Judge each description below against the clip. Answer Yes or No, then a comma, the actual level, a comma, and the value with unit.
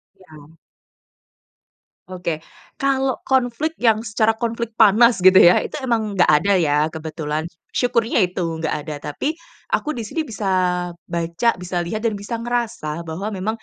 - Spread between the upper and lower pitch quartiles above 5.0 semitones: Yes, wide, 5.5 semitones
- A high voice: Yes, high, 210 Hz